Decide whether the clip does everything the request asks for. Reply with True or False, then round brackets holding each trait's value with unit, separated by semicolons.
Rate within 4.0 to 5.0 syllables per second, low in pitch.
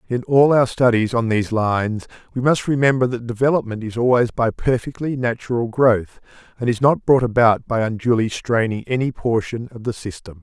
False (5.3 syllables/s; 120 Hz)